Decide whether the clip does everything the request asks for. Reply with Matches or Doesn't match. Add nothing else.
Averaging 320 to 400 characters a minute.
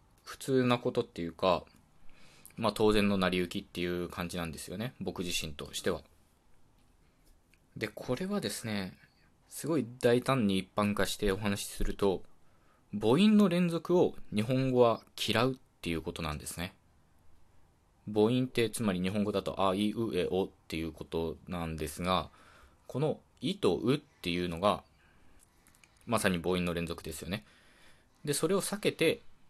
Doesn't match